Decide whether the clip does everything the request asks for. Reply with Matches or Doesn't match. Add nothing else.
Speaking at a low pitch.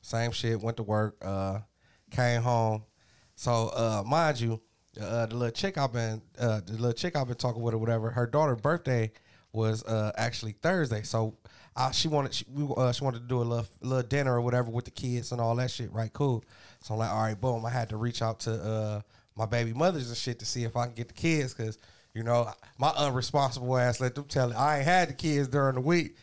Matches